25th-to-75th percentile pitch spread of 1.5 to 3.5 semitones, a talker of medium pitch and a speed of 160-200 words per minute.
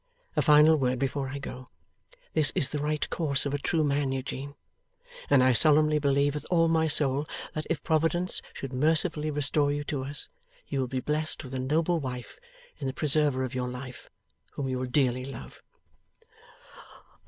Yes: average, 2.7 semitones; medium, 145 Hz; average, 180 wpm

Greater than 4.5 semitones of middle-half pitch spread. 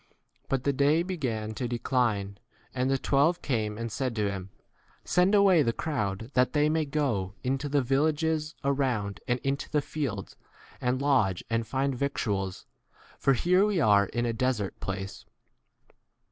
Yes: average, 5.1 semitones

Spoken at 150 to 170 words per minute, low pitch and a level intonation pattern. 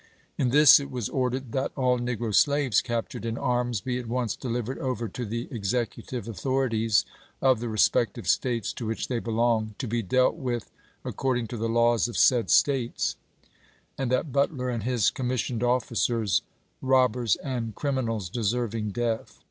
Yes: average, 165 wpm; low, 120 Hz; narrow, 2.0 semitones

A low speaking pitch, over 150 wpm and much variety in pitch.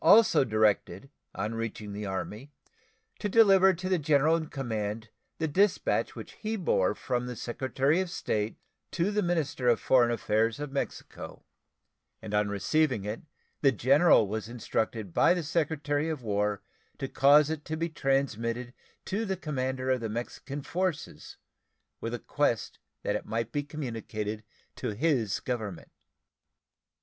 Yes: low, 130 Hz; average, 160 wpm; wide, 6.1 semitones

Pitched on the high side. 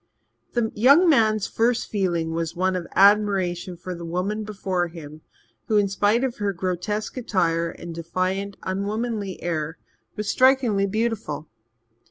Yes: high, 195 Hz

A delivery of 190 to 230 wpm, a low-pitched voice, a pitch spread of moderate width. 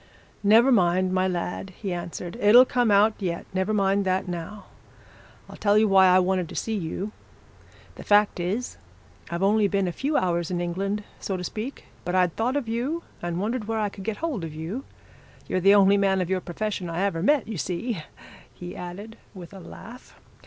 No: average, 200 wpm; high, 195 Hz; average, 3.3 semitones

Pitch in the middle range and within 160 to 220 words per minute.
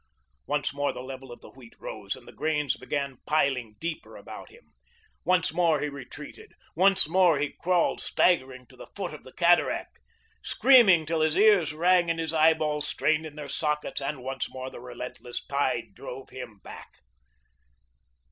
Yes: medium, 150 Hz; average, 170 wpm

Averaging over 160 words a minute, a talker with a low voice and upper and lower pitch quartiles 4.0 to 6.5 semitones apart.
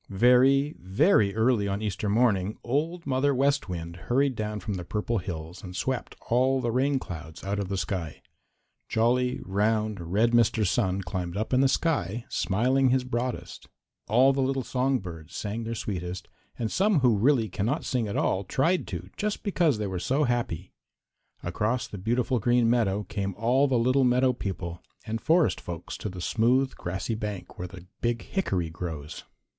Yes: average, 175 wpm; low, 115 Hz; average, 5.2 semitones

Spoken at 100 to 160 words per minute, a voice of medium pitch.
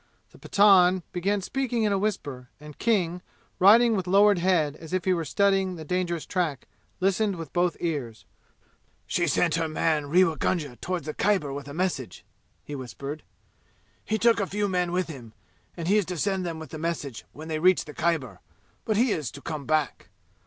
No: average, 195 wpm; medium, 175 Hz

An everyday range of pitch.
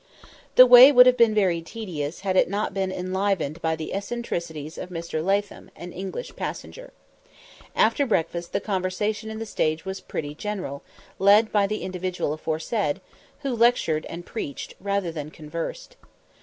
Yes: average, 4.5 semitones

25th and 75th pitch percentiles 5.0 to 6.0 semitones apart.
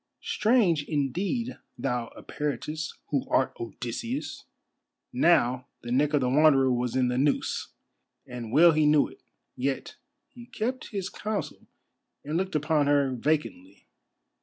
Yes: average, 5.3 semitones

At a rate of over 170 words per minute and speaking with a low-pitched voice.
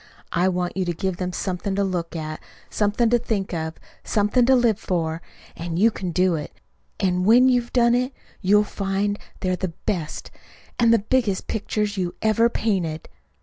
No: average, 190 wpm; high, 195 Hz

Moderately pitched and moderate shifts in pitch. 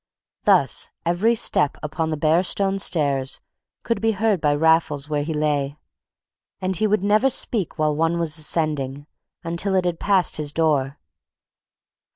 Yes: medium, 160 Hz; average, 4.4 semitones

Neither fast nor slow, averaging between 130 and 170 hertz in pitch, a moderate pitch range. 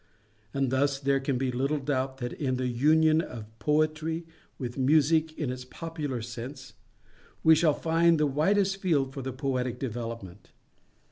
Yes: average, 155 wpm; low, 135 Hz; average, 3.6 semitones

